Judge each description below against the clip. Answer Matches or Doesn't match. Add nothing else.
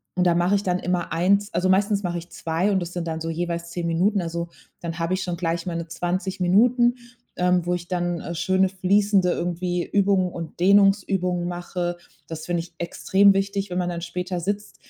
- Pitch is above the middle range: Doesn't match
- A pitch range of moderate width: Doesn't match